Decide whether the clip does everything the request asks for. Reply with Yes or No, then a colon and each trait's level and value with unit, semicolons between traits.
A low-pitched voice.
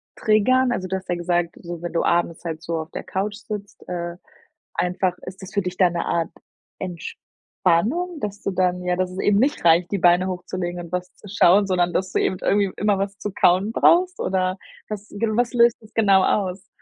No: medium, 185 Hz